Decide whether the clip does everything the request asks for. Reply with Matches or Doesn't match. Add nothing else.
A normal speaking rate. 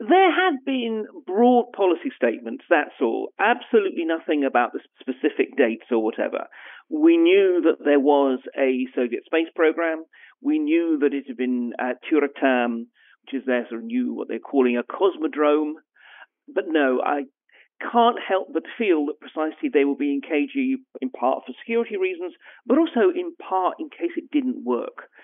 Matches